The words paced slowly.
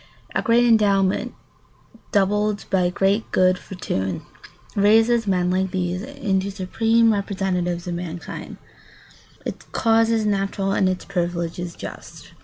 Yes: slow, 120 wpm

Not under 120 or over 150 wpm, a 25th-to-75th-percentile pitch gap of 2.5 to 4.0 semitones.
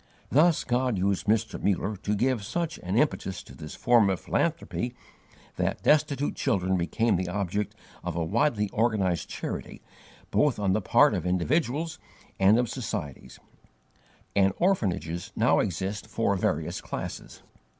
No: average, 140 wpm; average, 4.9 semitones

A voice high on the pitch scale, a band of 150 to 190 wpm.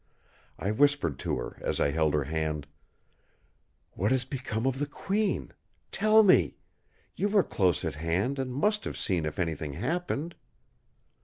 No: low, 120 Hz; average, 155 wpm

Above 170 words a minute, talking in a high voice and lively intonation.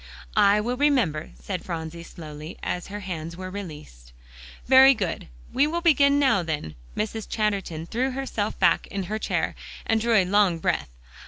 No: average, 165 wpm; high, 200 Hz; wide, 6.4 semitones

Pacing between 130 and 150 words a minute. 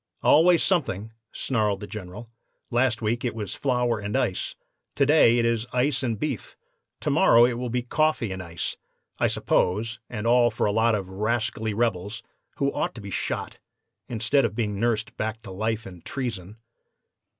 No: average, 175 wpm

